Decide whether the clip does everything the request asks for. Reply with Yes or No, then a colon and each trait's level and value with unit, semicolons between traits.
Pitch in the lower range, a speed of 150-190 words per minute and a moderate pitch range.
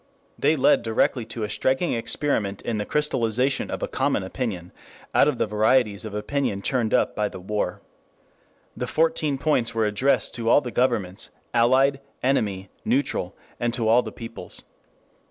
Yes: low, 115 Hz; average, 165 wpm; average, 3.9 semitones